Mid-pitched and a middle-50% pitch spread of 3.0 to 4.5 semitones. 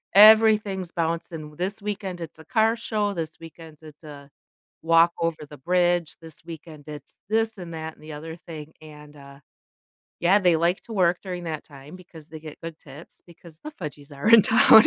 Yes: medium, 165 Hz; average, 3.5 semitones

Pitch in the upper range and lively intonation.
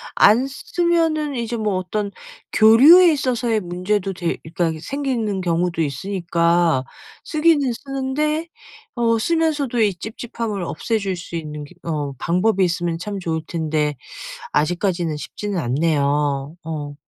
Yes: high, 195 Hz; wide, 6.6 semitones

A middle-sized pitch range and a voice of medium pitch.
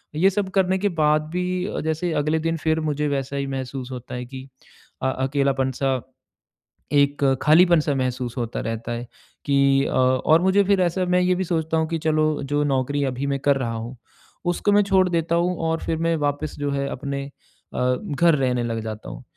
Yes: average, 4.1 semitones; medium, 145 Hz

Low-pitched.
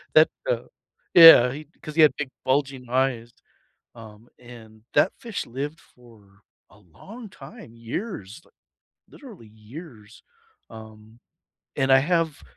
Yes: low, 125 Hz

